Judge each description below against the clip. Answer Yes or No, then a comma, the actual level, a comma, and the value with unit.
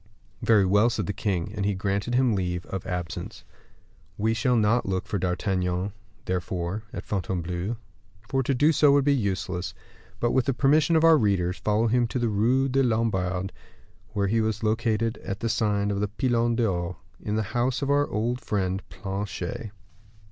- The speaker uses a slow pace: No, average, 180 wpm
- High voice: No, low, 105 Hz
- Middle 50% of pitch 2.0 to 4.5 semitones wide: Yes, average, 3.9 semitones